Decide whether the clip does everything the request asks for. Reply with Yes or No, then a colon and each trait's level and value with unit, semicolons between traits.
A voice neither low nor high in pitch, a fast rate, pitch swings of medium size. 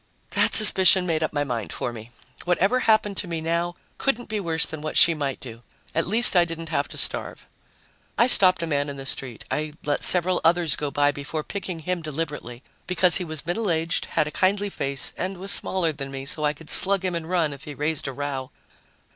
Yes: medium, 165 Hz; fast, 220 wpm; average, 4.1 semitones